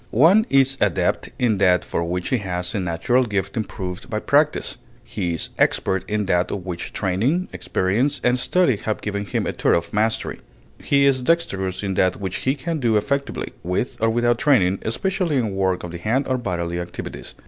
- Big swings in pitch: Yes, wide, 6.0 semitones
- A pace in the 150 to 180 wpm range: No, average, 190 wpm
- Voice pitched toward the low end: Yes, low, 105 Hz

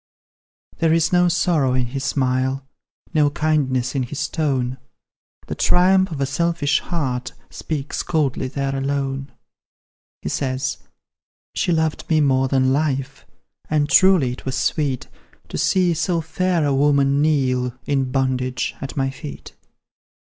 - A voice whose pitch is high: No, medium, 140 Hz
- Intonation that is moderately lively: Yes, average, 3.1 semitones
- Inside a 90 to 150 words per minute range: Yes, average, 140 wpm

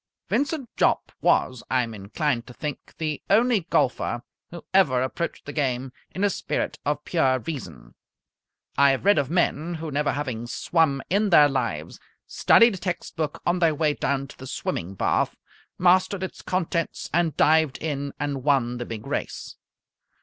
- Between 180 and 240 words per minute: No, average, 170 wpm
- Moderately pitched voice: Yes, medium, 145 Hz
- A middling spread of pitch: Yes, average, 5.0 semitones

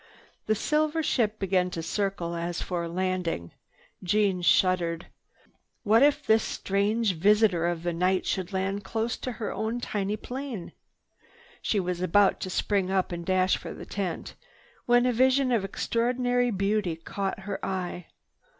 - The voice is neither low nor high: No, high, 195 Hz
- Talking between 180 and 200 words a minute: No, average, 155 wpm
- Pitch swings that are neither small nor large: Yes, average, 3.7 semitones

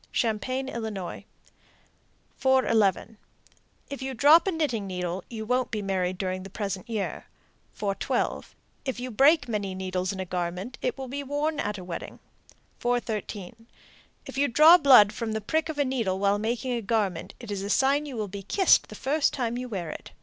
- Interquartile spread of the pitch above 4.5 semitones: Yes, average, 5.2 semitones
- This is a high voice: Yes, high, 225 Hz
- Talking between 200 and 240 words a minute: No, average, 185 wpm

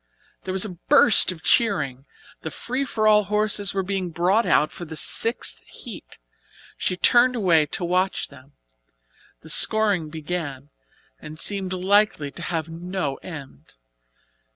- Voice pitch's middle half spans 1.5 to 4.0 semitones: No, average, 4.6 semitones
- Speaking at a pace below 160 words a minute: Yes, average, 145 wpm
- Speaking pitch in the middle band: Yes, medium, 180 Hz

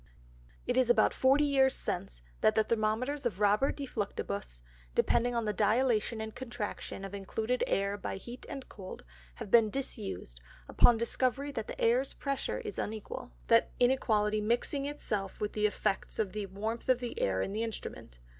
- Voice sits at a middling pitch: No, high, 220 Hz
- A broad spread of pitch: No, average, 3.7 semitones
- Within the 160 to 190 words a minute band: Yes, average, 175 wpm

